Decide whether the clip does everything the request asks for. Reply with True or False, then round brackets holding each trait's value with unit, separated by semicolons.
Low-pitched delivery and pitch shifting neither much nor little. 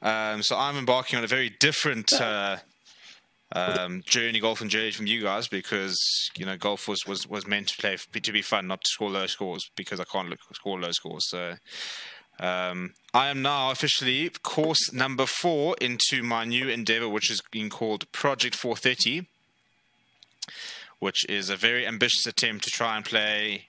True (110 Hz; 3.5 semitones)